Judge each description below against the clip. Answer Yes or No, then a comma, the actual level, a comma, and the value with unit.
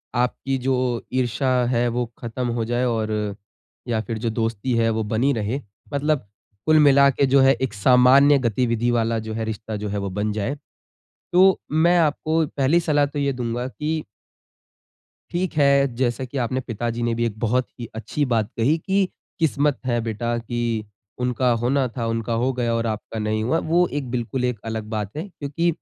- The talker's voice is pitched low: Yes, low, 125 Hz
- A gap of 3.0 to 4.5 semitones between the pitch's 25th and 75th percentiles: Yes, average, 3.6 semitones